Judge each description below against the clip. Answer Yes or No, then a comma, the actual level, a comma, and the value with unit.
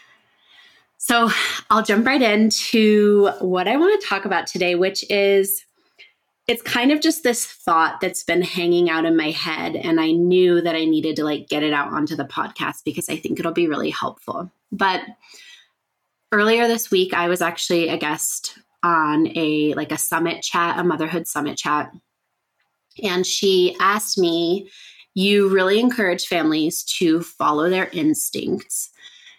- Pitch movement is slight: No, average, 4.4 semitones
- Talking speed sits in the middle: Yes, average, 160 wpm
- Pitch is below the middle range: No, medium, 185 Hz